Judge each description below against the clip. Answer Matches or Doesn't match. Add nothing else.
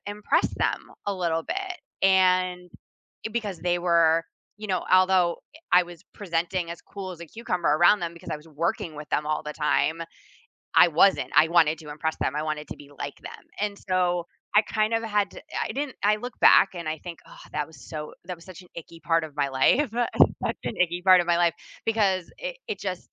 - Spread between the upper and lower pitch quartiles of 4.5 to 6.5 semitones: Doesn't match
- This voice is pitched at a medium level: Matches